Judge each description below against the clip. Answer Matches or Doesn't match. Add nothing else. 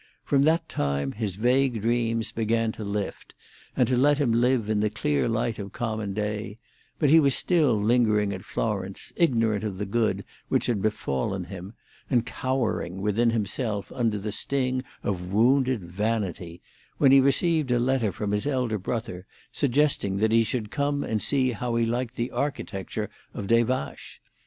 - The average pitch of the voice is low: Matches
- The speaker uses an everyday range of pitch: Matches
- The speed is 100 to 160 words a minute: Doesn't match